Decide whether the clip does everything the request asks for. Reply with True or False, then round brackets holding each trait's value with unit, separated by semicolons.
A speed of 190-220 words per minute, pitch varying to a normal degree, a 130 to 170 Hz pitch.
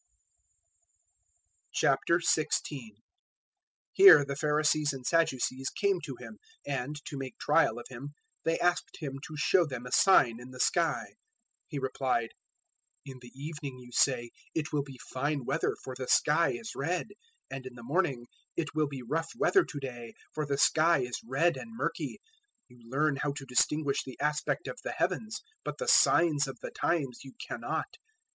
False (170 wpm; 3.3 semitones; 140 Hz)